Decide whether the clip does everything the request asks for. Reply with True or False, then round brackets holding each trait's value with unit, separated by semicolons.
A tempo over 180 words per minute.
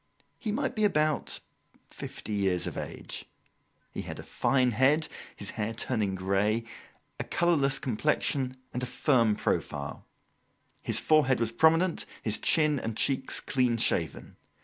False (140 wpm)